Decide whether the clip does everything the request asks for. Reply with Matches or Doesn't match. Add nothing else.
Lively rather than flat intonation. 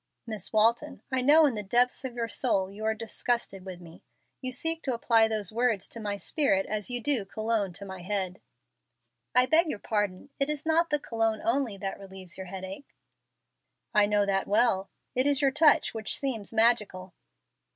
Doesn't match